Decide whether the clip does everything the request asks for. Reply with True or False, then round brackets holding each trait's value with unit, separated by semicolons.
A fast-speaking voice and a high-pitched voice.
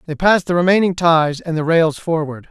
False (215 wpm; 165 Hz)